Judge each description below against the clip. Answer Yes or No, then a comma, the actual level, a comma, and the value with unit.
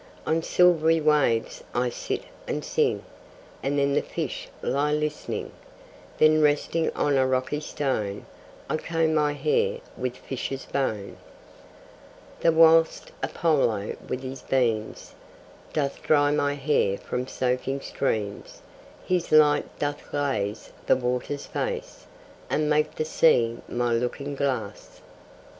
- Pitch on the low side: No, medium, 145 Hz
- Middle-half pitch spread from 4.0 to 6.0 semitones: No, average, 3.5 semitones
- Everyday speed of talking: No, slow, 125 wpm